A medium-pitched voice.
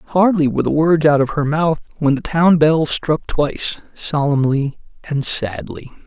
Yes: medium, 150 Hz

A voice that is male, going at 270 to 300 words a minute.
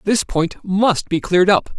No: male; average, 200 wpm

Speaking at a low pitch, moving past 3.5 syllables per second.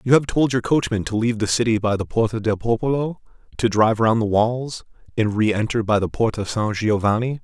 Yes: low, 115 Hz; 5.7 syllables/s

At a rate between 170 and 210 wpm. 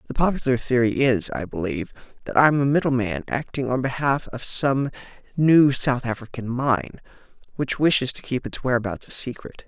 Yes: average, 175 wpm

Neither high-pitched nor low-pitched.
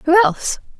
No: very high, 255 Hz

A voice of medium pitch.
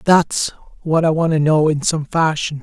Yes: medium, 155 Hz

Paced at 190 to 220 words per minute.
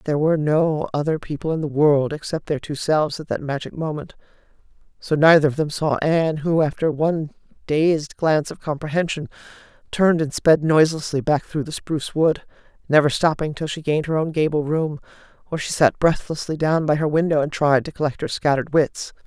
Yes: average, 195 wpm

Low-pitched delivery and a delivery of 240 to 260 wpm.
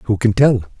No: low, 110 Hz; fast, 225 wpm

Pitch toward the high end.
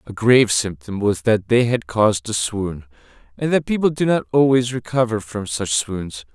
No: low, 120 Hz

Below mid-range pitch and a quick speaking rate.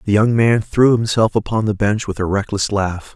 Yes: low, 105 Hz; fast, 230 wpm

